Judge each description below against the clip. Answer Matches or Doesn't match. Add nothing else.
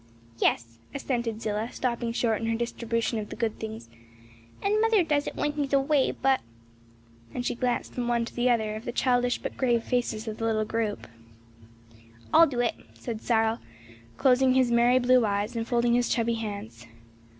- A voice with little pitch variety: Matches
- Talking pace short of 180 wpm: Doesn't match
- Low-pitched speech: Doesn't match